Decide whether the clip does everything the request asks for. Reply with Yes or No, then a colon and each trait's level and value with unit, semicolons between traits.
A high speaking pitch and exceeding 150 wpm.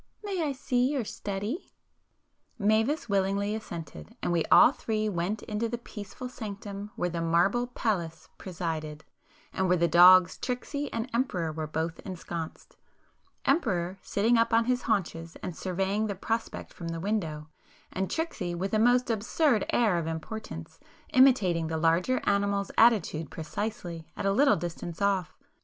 No: high, 200 Hz; average, 145 wpm